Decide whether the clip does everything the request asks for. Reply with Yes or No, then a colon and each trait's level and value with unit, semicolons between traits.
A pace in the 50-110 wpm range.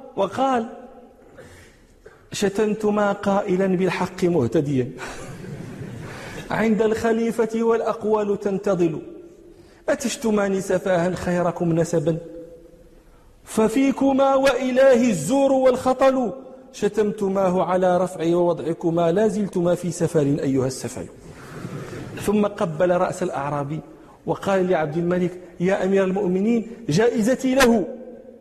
Yes: average, 80 wpm